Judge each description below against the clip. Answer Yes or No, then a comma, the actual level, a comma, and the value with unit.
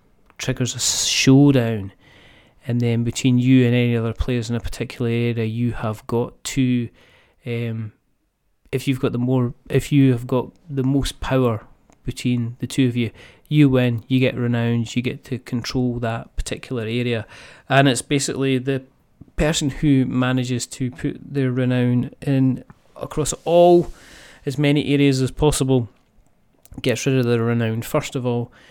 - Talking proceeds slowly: No, average, 160 wpm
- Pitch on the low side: Yes, low, 125 Hz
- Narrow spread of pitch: Yes, narrow, 2.2 semitones